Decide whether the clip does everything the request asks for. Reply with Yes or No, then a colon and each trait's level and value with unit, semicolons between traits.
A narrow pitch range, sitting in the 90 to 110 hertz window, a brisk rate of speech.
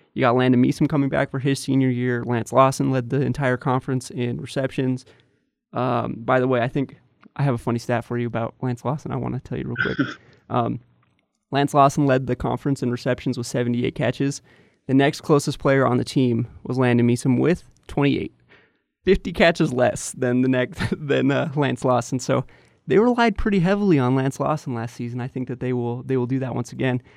No: narrow, 2.2 semitones; low, 130 Hz; fast, 210 wpm